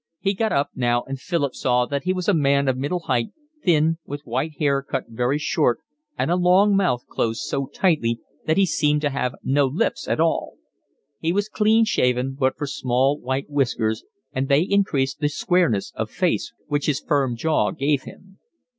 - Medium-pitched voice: Yes, medium, 145 Hz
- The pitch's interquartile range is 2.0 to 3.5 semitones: No, average, 4.4 semitones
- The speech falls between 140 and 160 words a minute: No, average, 190 wpm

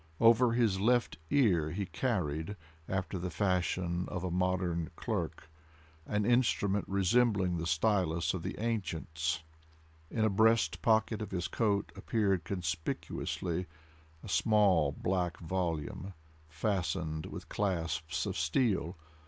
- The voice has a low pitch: Yes, very low, 95 Hz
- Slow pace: Yes, slow, 120 wpm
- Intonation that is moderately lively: Yes, average, 4.0 semitones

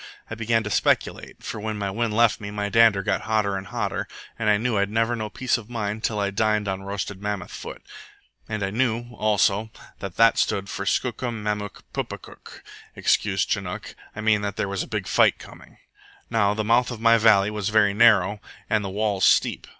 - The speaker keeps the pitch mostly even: Yes, narrow, 2.0 semitones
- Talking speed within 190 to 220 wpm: Yes, average, 200 wpm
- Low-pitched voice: Yes, low, 105 Hz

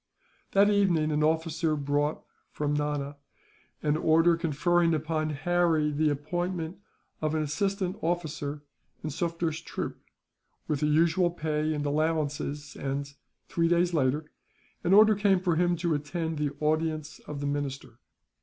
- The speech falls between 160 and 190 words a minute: No, average, 140 wpm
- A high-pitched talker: No, medium, 155 Hz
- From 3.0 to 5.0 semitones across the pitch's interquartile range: No, narrow, 2.6 semitones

